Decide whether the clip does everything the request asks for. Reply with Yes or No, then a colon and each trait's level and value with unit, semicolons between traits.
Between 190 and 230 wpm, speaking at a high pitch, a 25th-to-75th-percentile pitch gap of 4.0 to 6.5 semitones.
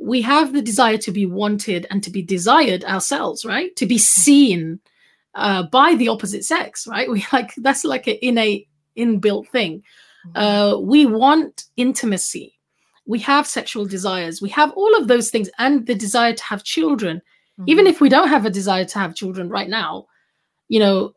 No: average, 180 wpm; high, 225 Hz; wide, 5.4 semitones